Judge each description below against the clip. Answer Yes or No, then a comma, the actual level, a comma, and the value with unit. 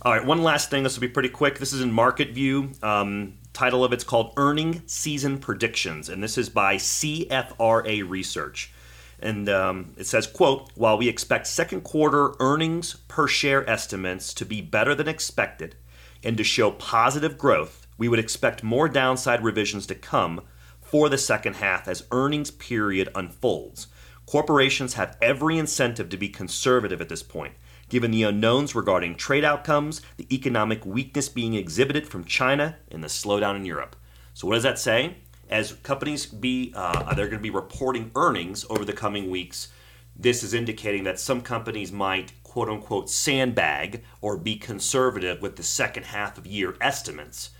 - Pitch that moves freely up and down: Yes, wide, 6.1 semitones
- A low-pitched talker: Yes, low, 115 Hz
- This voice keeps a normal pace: Yes, average, 170 wpm